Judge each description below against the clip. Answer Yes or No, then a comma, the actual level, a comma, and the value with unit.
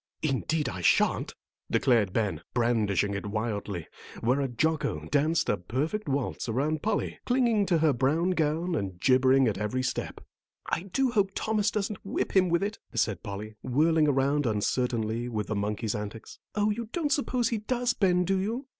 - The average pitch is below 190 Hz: Yes, medium, 140 Hz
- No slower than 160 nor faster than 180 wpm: Yes, average, 170 wpm